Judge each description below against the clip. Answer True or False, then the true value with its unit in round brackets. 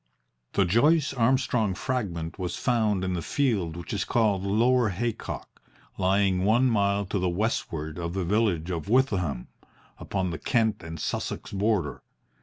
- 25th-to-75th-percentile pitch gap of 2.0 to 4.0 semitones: False (4.5 semitones)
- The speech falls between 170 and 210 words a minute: False (150 wpm)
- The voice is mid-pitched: False (100 Hz)